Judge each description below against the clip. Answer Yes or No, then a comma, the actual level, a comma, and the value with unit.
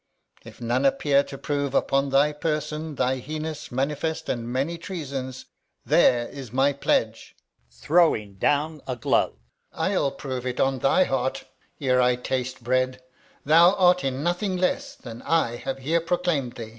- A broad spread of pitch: No, average, 3.6 semitones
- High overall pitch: No, low, 135 Hz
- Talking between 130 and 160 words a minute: Yes, average, 155 wpm